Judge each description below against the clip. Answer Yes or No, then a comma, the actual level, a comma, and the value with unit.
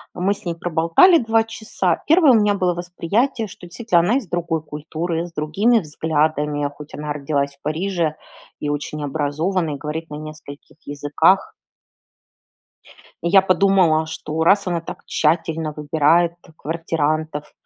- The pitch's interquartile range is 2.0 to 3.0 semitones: No, average, 3.6 semitones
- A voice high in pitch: No, medium, 165 Hz